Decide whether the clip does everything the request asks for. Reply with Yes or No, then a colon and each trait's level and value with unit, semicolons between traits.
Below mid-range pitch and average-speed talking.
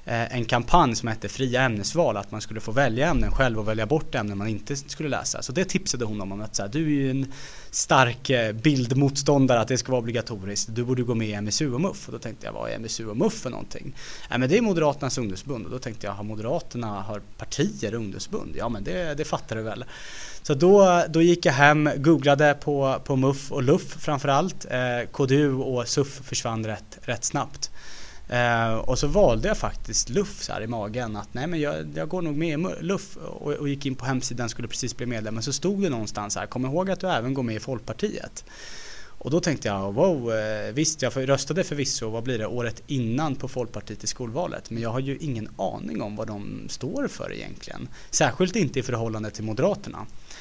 No: low, 125 Hz; fast, 215 wpm